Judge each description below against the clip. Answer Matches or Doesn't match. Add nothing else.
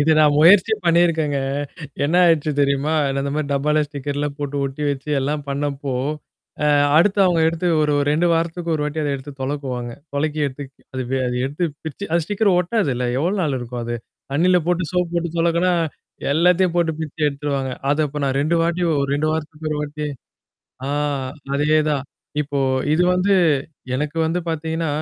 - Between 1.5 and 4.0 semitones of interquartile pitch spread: Matches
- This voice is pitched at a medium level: Matches